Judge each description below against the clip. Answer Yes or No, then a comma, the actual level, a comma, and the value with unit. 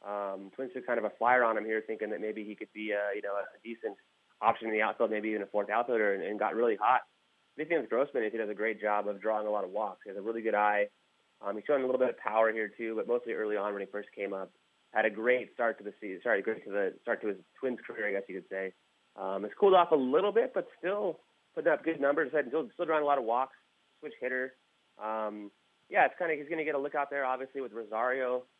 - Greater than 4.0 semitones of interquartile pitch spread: No, average, 3.7 semitones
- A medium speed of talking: No, fast, 280 wpm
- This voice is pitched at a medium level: No, low, 110 Hz